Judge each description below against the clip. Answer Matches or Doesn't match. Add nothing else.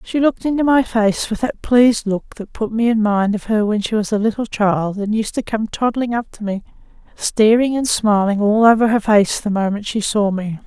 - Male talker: Doesn't match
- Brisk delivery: Matches